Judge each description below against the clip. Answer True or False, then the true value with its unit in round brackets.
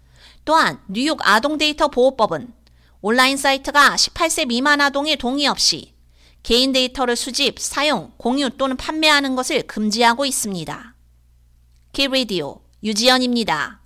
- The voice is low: False (255 Hz)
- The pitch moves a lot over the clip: False (5.0 semitones)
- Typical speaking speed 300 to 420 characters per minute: False (250 characters per minute)